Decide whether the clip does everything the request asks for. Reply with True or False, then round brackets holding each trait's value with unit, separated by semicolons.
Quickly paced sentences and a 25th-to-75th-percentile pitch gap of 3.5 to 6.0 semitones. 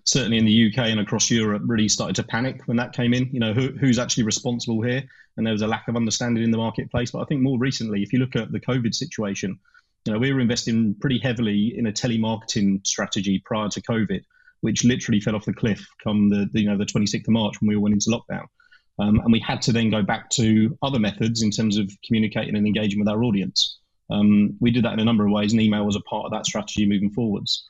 False (255 wpm; 2.5 semitones)